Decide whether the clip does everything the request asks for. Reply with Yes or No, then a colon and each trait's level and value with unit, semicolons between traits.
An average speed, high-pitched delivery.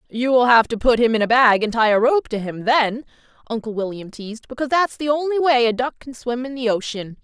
No: fast, 255 wpm; high, 240 Hz